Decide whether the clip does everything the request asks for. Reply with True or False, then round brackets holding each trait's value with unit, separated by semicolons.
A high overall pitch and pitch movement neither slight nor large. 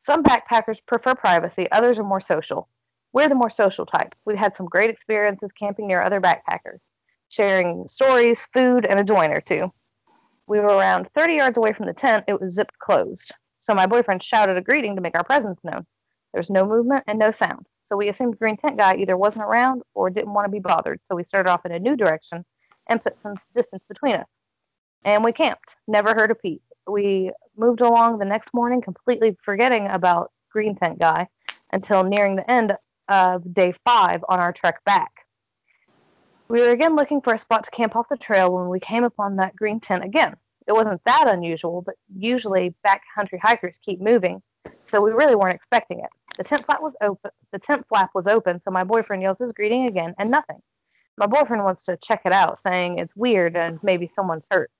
True (210 Hz; 4.0 semitones)